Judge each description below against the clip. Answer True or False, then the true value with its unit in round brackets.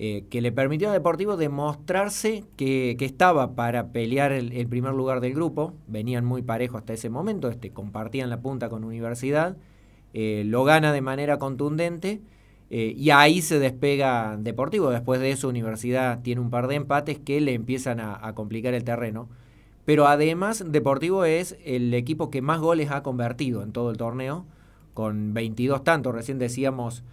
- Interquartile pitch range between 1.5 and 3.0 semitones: False (3.9 semitones)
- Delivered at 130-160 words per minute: False (175 wpm)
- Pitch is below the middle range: True (130 Hz)